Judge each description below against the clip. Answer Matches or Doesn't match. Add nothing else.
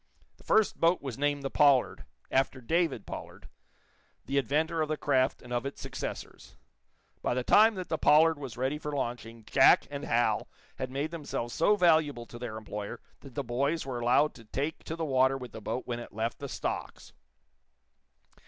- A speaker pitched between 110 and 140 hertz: Matches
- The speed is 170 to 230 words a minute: Matches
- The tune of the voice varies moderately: Matches